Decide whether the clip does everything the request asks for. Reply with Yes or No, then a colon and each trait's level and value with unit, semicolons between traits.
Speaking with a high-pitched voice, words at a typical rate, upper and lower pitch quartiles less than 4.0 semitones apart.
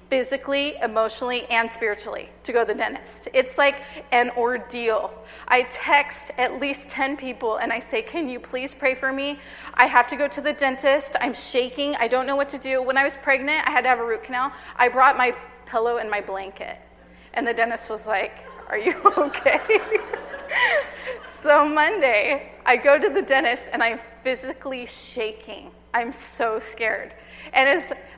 Yes: very high, 260 Hz; average, 180 wpm; average, 3.3 semitones